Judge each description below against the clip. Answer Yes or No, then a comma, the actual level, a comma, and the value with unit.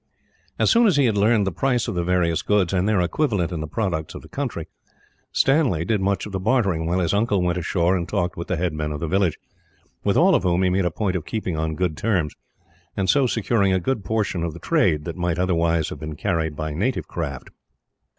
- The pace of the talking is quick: Yes, fast, 240 wpm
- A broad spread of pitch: No, average, 3.8 semitones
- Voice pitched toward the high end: No, very low, 90 Hz